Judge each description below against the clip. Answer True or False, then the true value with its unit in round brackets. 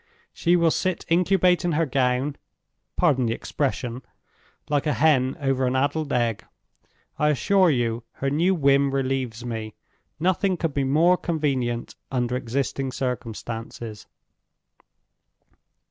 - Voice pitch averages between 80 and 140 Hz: True (135 Hz)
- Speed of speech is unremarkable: False (115 wpm)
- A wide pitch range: False (4.4 semitones)